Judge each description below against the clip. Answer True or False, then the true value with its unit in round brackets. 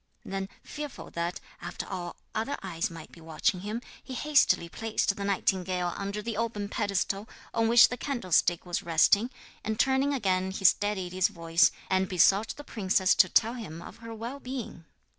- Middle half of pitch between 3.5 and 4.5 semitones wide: True (4.1 semitones)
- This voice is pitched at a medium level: False (200 Hz)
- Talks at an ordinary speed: True (175 wpm)